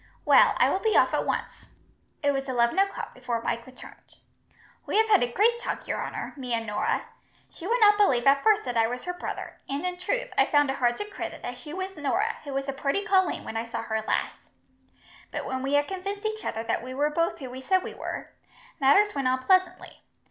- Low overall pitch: No, very high, 285 Hz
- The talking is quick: Yes, fast, 235 wpm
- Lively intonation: Yes, wide, 7.5 semitones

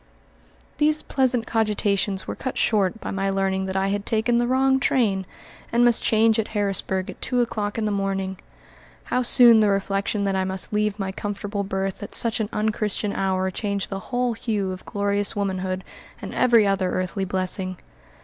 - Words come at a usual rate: Yes, average, 180 wpm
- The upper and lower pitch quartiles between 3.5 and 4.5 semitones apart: No, average, 2.7 semitones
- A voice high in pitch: Yes, high, 205 Hz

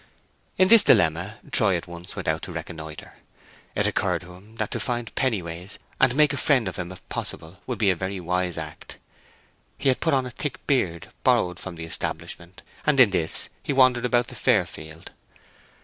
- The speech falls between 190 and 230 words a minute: Yes, average, 195 wpm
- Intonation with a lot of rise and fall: Yes, wide, 6.6 semitones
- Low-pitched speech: Yes, very low, 95 Hz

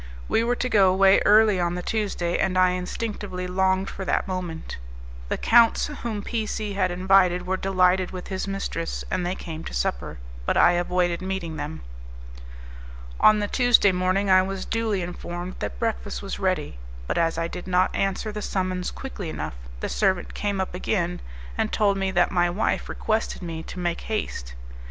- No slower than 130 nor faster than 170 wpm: No, average, 185 wpm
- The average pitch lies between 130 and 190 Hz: Yes, medium, 185 Hz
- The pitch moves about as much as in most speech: No, narrow, 2.3 semitones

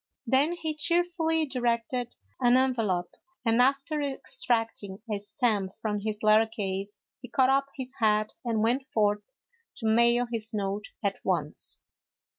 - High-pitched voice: Yes, high, 230 Hz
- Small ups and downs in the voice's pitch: No, average, 4.0 semitones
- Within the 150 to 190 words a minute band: No, average, 140 wpm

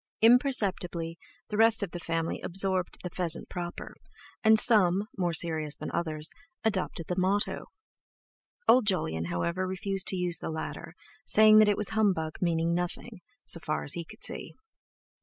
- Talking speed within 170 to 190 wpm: No, average, 160 wpm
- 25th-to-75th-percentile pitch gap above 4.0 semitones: No, average, 3.7 semitones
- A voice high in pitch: No, medium, 180 Hz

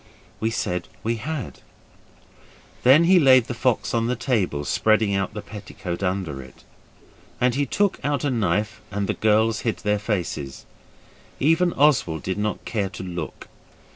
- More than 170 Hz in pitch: No, low, 110 Hz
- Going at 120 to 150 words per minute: No, average, 160 wpm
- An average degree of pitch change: Yes, average, 4.9 semitones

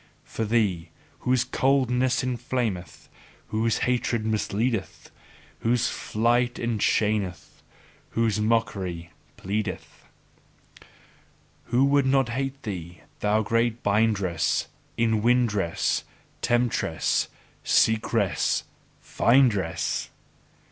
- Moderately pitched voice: No, low, 115 Hz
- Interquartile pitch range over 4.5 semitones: No, average, 3.1 semitones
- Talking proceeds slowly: Yes, slow, 75 wpm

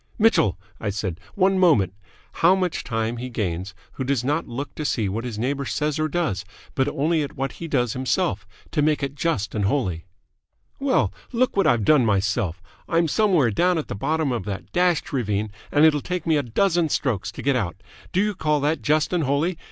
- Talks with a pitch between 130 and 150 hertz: Yes, medium, 140 Hz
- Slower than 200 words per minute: No, fast, 205 wpm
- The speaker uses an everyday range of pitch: No, wide, 7.0 semitones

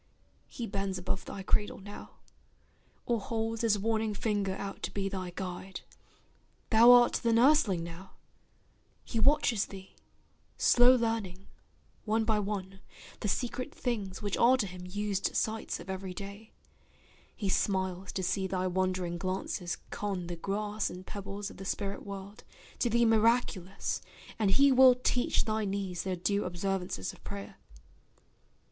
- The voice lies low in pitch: No, high, 200 Hz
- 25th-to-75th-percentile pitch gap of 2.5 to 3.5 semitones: Yes, average, 2.9 semitones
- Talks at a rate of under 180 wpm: Yes, average, 150 wpm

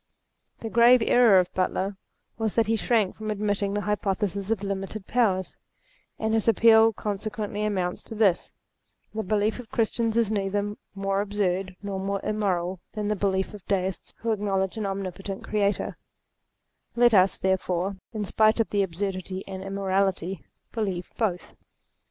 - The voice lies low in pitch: No, high, 200 Hz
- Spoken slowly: No, average, 155 wpm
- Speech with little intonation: Yes, narrow, 2.1 semitones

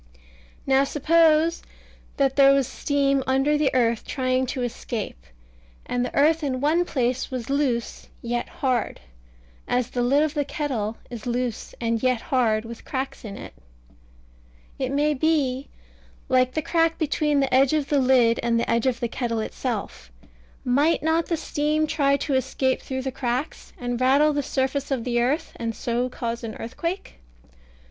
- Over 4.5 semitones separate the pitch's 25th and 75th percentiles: No, average, 3.2 semitones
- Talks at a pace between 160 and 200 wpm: Yes, average, 170 wpm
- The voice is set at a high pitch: Yes, very high, 260 Hz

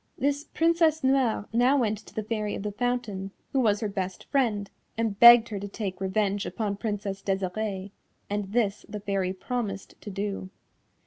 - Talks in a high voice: Yes, high, 210 Hz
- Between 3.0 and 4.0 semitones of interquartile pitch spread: Yes, average, 3.3 semitones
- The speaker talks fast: No, average, 175 wpm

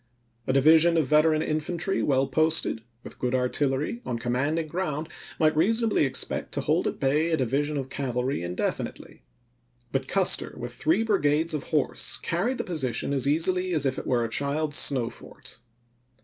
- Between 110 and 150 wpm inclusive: No, average, 165 wpm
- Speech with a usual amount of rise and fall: Yes, average, 3.6 semitones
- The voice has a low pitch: No, medium, 150 Hz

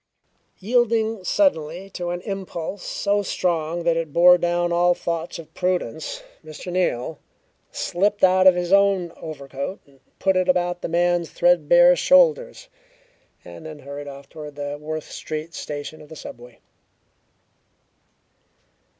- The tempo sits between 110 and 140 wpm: Yes, slow, 135 wpm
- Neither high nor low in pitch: Yes, medium, 175 Hz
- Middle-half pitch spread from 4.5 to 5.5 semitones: No, average, 3.5 semitones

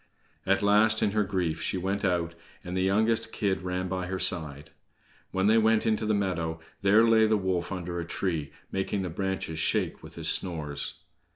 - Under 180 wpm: No, average, 190 wpm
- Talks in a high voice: No, very low, 95 Hz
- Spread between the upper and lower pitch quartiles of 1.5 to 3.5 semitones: Yes, average, 3.1 semitones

